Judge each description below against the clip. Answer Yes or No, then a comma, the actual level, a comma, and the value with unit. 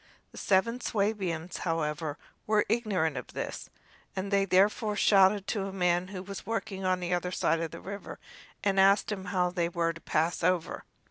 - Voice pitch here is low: No, high, 190 Hz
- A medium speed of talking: Yes, average, 185 wpm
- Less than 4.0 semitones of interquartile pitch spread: Yes, narrow, 2.6 semitones